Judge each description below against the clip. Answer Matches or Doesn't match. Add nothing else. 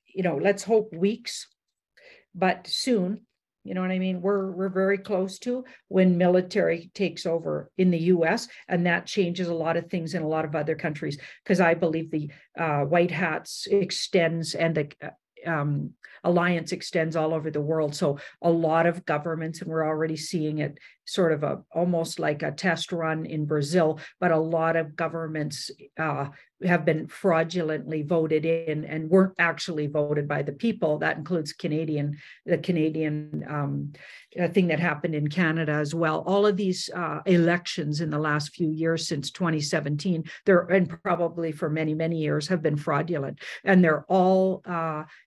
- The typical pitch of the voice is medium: Matches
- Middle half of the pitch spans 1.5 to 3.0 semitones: Matches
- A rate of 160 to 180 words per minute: Matches